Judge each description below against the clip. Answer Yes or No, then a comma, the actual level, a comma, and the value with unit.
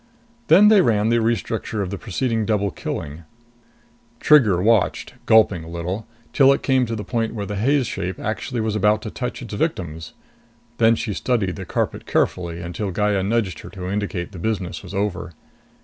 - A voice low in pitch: Yes, low, 105 Hz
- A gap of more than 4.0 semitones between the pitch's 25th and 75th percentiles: No, average, 3.7 semitones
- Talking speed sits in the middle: Yes, average, 180 wpm